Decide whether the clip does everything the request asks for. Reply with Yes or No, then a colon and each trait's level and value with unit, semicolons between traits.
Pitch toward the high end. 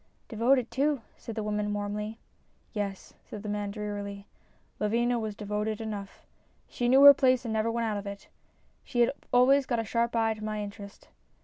Yes: high, 220 Hz